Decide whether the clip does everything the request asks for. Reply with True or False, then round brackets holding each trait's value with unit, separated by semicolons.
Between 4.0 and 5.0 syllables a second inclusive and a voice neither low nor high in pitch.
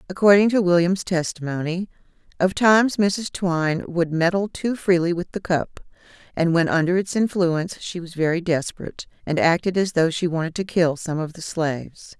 False (5.2 syllables/s; 175 Hz)